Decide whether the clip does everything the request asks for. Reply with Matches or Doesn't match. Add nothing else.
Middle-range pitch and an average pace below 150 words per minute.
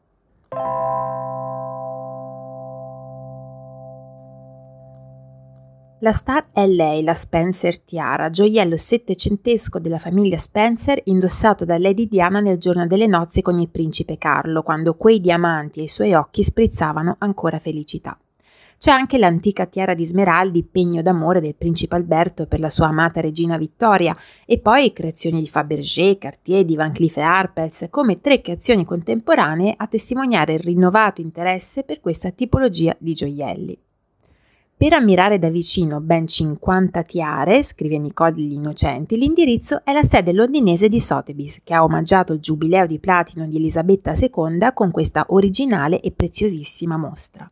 Matches